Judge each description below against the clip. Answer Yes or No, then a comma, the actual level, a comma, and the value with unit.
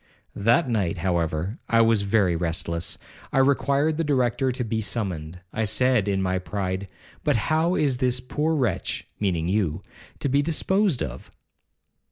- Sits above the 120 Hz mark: No, low, 110 Hz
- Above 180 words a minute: No, average, 155 wpm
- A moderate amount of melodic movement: No, wide, 6.5 semitones